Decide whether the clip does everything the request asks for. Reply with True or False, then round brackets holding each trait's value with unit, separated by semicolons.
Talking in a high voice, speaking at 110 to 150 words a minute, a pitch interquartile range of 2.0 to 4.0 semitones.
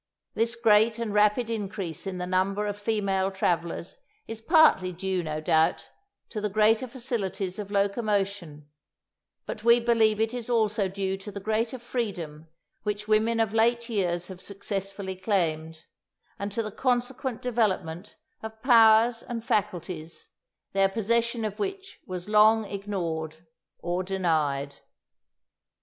True (205 Hz; 135 wpm; 3.4 semitones)